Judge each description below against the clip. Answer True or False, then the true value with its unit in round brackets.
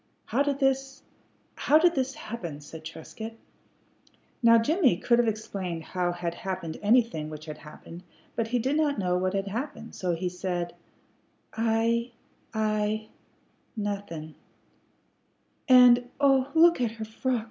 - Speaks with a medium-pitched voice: False (220 Hz)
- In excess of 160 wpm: False (140 wpm)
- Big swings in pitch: True (5.8 semitones)